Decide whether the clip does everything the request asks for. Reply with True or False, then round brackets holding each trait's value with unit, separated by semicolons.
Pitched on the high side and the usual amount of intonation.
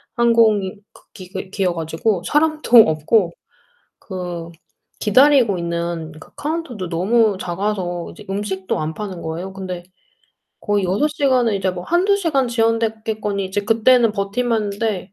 True (205 Hz; 4.2 semitones)